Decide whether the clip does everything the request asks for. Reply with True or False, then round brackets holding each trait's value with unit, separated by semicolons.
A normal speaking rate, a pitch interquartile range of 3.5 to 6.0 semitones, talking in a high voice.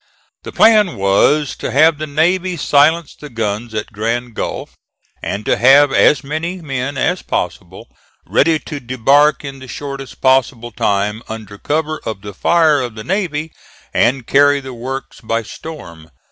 False (160 wpm; 5.2 semitones; 135 Hz)